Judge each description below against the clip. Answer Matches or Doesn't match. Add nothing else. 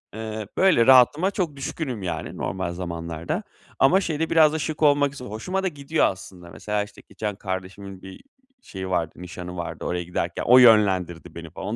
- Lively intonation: Matches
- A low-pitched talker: Matches